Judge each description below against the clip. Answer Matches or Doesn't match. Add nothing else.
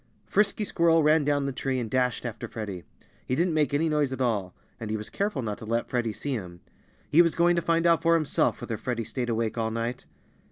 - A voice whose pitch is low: Matches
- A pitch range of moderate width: Doesn't match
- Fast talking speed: Matches